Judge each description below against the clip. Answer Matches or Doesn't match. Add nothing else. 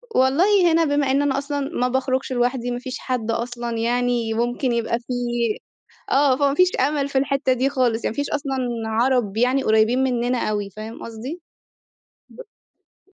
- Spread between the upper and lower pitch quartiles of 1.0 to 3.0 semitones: Matches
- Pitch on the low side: Doesn't match